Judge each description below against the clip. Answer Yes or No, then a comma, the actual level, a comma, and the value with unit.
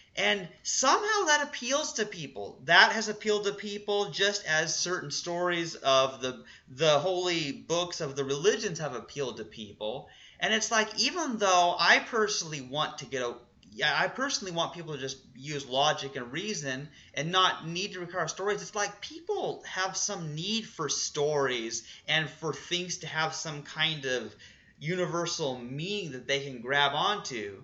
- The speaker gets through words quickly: No, average, 170 wpm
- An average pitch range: No, wide, 6.4 semitones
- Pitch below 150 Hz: No, medium, 170 Hz